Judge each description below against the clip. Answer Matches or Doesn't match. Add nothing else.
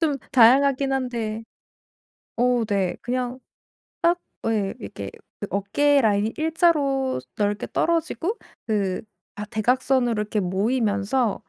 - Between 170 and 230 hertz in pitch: Doesn't match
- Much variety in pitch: Doesn't match